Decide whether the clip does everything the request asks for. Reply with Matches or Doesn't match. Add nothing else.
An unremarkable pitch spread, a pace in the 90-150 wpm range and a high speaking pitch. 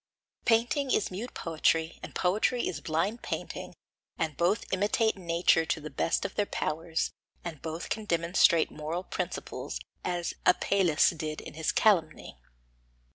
Doesn't match